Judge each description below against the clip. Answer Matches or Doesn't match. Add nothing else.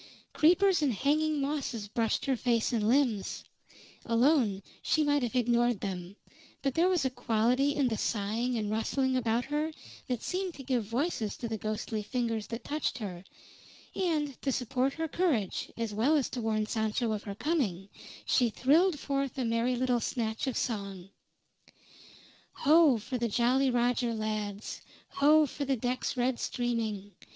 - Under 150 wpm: Doesn't match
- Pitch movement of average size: Matches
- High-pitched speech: Matches